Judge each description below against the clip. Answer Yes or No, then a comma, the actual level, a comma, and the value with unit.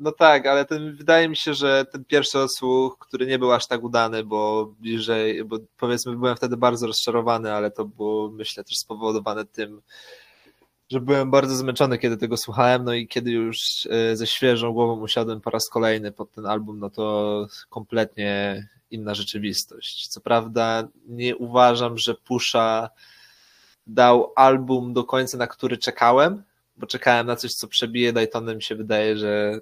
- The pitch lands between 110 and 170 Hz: Yes, low, 115 Hz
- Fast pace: Yes, fast, 165 wpm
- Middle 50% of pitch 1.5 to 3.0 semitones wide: Yes, narrow, 2.4 semitones